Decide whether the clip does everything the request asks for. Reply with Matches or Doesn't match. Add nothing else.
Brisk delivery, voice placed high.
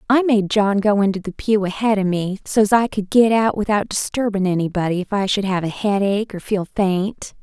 Matches